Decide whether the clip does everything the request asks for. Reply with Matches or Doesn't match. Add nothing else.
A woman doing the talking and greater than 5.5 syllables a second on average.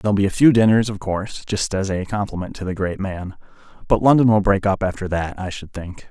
Doesn't match